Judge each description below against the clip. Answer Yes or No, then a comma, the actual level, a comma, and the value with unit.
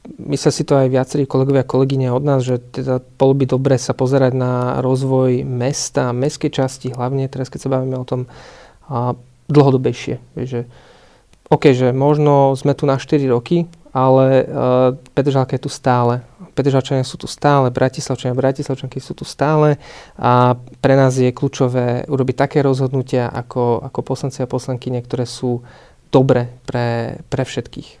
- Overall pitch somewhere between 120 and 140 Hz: Yes, low, 130 Hz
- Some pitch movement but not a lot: No, narrow, 1.6 semitones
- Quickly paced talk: No, average, 155 wpm